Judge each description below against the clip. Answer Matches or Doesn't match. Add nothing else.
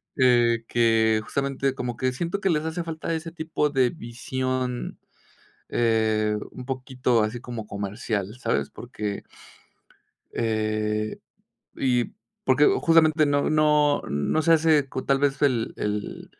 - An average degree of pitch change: Matches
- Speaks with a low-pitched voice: Matches